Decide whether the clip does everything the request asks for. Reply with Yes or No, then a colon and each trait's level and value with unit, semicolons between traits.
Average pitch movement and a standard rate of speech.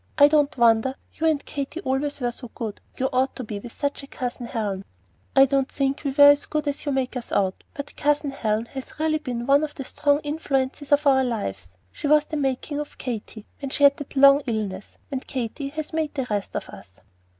No: average, 3.2 semitones; fast, 225 wpm